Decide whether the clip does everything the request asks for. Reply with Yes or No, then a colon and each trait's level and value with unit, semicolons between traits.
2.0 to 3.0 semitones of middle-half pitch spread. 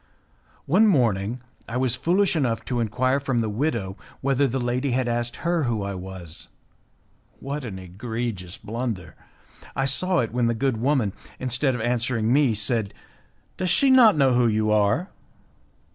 No: average, 3.9 semitones